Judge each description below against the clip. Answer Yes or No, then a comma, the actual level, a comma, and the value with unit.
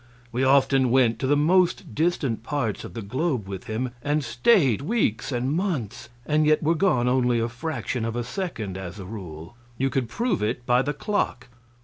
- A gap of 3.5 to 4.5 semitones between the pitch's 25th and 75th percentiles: No, average, 4.9 semitones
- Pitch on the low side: Yes, low, 130 Hz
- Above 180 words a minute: Yes, average, 195 wpm